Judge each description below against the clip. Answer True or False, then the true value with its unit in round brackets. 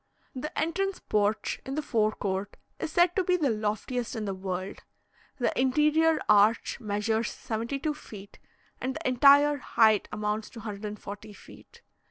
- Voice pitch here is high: True (230 Hz)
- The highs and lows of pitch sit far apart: True (5.7 semitones)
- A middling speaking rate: True (150 wpm)